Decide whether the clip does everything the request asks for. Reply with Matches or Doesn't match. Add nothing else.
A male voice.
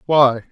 Matches